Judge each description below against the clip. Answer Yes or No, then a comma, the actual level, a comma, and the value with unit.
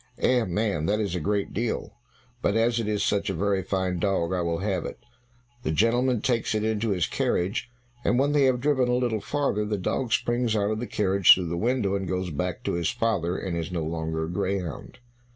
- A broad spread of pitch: No, average, 4.4 semitones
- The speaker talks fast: Yes, fast, 225 wpm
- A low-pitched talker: Yes, low, 100 Hz